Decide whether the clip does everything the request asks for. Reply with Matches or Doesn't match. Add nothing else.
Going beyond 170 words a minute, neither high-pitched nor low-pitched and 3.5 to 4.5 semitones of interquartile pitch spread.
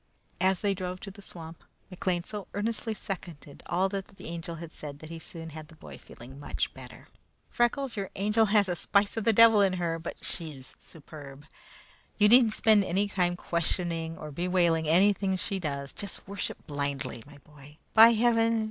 Matches